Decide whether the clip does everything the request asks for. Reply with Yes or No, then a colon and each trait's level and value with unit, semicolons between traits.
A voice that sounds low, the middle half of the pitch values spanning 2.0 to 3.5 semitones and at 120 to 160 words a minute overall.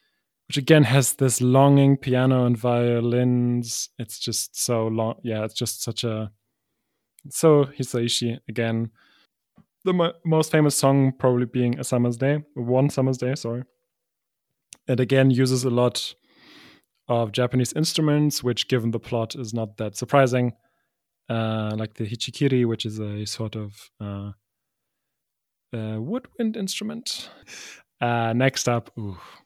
Yes: low, 125 Hz; average, 3.0 semitones; slow, 135 wpm